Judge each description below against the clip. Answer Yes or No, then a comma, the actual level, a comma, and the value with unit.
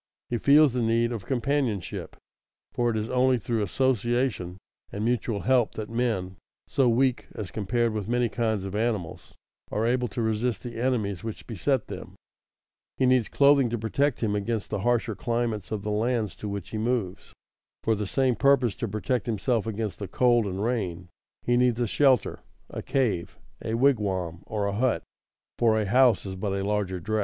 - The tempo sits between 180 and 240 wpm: Yes, average, 185 wpm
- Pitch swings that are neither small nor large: Yes, average, 3.2 semitones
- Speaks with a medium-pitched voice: No, low, 115 Hz